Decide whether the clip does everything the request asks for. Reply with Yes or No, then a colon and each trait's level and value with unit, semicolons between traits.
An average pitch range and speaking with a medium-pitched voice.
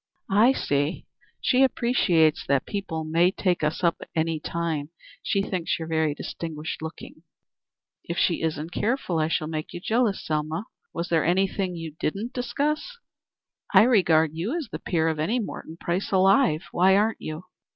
Yes: average, 4.1 semitones; medium, 170 Hz